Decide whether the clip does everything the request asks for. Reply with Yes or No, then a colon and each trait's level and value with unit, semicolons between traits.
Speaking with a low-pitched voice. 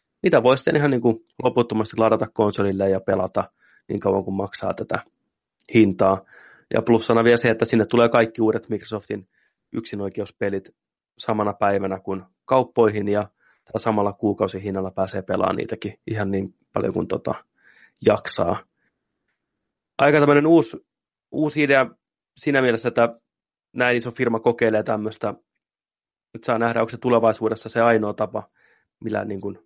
Yes: low, 110 Hz